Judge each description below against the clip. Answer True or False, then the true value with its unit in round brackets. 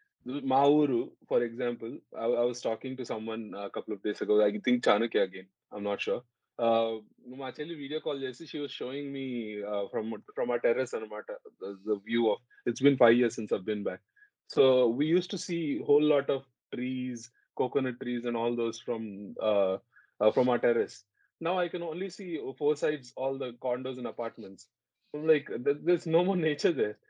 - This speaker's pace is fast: True (190 wpm)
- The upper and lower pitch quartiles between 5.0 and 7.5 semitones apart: True (5.6 semitones)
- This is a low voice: True (130 Hz)